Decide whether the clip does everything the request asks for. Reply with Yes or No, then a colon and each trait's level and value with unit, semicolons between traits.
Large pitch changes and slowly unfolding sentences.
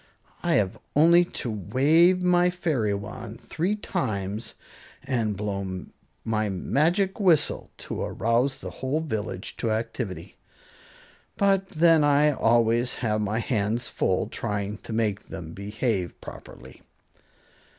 Yes: wide, 7.2 semitones; slow, 120 wpm